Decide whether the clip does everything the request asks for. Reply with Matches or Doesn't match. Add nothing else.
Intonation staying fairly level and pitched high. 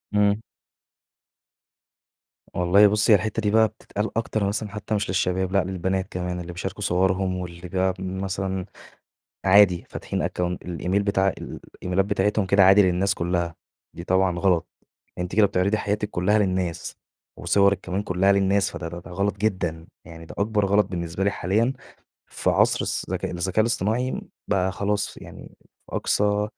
Doesn't match